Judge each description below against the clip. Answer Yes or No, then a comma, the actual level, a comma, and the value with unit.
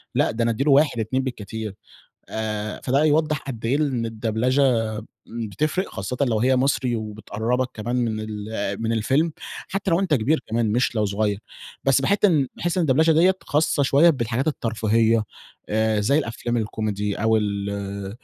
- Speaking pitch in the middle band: No, low, 115 Hz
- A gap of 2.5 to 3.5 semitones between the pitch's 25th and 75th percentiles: No, average, 4.3 semitones